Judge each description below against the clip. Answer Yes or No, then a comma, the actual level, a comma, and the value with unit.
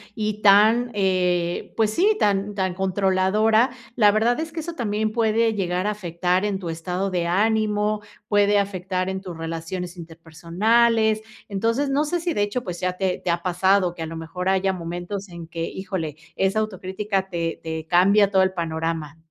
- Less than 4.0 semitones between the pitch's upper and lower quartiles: Yes, average, 3.4 semitones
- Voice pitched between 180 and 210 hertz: Yes, high, 190 Hz